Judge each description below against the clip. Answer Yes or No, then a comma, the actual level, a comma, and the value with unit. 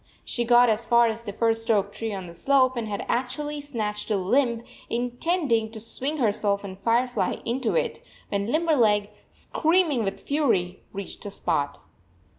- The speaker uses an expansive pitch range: No, average, 3.9 semitones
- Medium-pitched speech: No, high, 230 Hz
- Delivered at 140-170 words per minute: Yes, average, 165 wpm